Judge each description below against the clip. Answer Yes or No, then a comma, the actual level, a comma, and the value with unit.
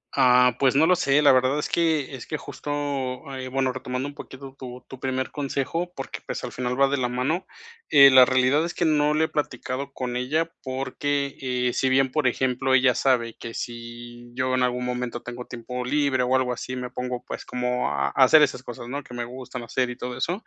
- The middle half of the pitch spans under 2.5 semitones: Yes, narrow, 1.9 semitones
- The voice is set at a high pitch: No, low, 130 Hz